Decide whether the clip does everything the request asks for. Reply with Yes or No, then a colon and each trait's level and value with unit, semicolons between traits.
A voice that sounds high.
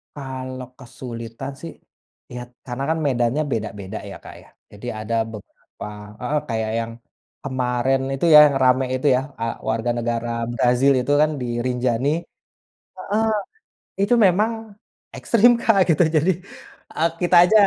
No: low, 130 Hz